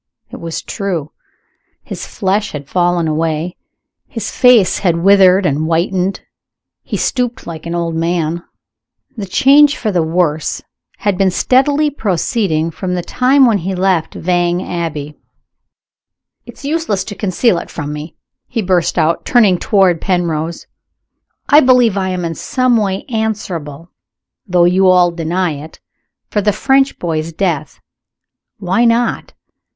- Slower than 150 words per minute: Yes, average, 140 wpm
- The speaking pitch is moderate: Yes, medium, 180 Hz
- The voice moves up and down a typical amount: Yes, average, 4.3 semitones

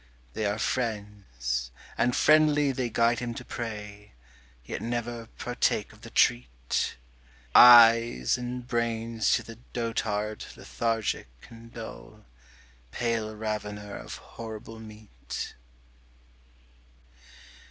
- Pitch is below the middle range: Yes, low, 115 Hz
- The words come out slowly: Yes, slow, 100 wpm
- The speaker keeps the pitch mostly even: Yes, narrow, 2.3 semitones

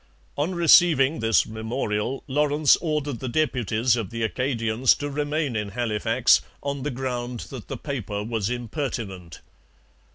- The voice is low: Yes, low, 125 Hz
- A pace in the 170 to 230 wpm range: No, slow, 135 wpm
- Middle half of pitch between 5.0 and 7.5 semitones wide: No, average, 4.5 semitones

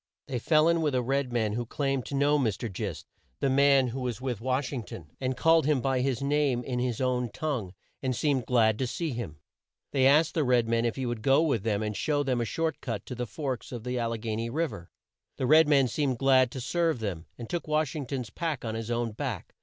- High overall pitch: No, low, 130 Hz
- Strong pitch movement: No, average, 3.5 semitones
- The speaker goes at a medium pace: No, fast, 255 wpm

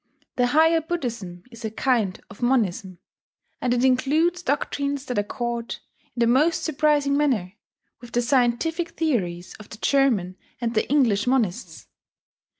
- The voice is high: Yes, high, 245 Hz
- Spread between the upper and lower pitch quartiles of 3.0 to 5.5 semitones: Yes, average, 4.8 semitones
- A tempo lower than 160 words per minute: Yes, average, 145 wpm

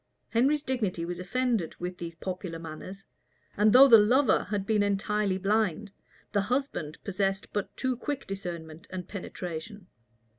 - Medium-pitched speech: No, high, 200 Hz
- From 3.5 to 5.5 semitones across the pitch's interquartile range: Yes, average, 3.9 semitones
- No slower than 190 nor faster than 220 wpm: No, average, 145 wpm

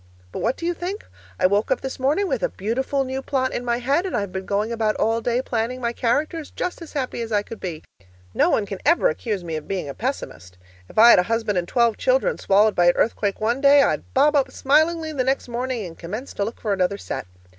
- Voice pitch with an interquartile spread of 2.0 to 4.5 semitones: No, average, 5.2 semitones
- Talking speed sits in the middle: No, fast, 250 wpm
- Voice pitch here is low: No, high, 235 Hz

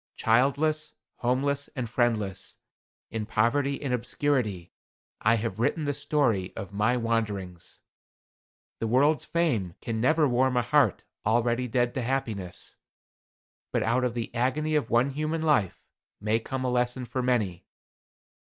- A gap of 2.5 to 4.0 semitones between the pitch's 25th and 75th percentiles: Yes, average, 3.7 semitones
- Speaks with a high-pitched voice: No, low, 120 Hz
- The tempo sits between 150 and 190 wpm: No, average, 140 wpm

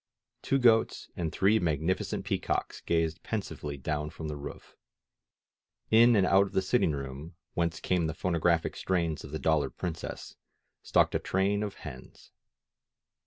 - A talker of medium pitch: No, very low, 85 Hz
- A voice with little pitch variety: No, average, 3.9 semitones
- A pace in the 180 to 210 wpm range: No, average, 155 wpm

